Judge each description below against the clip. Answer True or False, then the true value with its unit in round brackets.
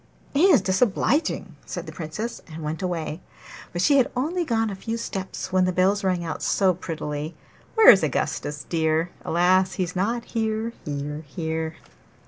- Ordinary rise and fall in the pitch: False (5.7 semitones)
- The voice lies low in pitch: False (185 Hz)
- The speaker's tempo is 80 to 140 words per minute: False (165 wpm)